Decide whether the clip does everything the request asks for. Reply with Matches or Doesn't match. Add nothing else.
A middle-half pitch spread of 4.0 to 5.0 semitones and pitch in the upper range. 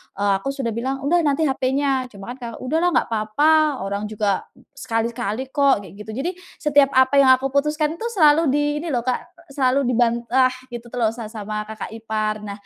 Matches